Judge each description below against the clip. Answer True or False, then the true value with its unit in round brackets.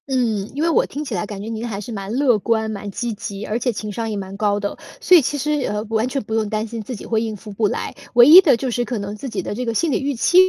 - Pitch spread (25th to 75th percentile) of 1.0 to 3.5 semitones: True (3.2 semitones)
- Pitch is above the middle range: True (225 Hz)